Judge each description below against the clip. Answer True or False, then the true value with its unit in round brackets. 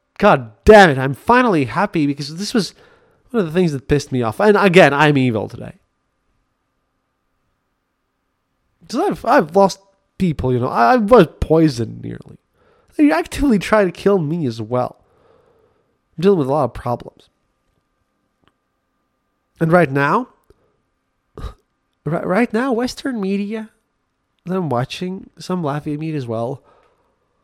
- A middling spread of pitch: False (7.5 semitones)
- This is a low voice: False (185 Hz)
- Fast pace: False (140 wpm)